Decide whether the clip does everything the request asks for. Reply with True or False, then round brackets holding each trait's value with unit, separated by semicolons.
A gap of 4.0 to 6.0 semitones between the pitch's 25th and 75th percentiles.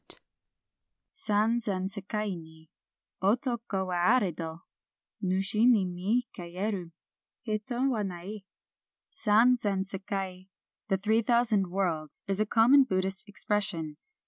False (3.1 semitones)